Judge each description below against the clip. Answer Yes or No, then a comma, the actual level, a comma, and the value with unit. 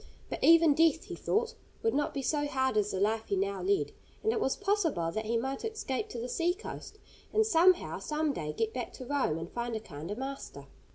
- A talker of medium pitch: No, very high, 280 Hz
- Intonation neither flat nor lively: No, wide, 8.6 semitones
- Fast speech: Yes, fast, 225 wpm